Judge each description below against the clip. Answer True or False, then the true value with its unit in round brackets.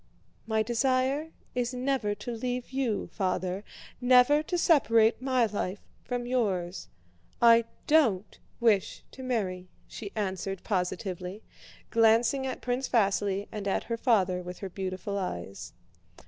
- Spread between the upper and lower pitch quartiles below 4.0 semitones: False (4.6 semitones)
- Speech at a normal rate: False (130 wpm)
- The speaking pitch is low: False (225 Hz)